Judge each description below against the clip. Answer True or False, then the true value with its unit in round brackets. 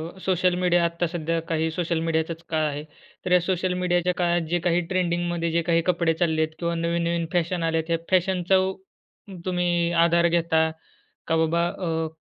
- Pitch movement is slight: True (1.3 semitones)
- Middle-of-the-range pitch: True (170 Hz)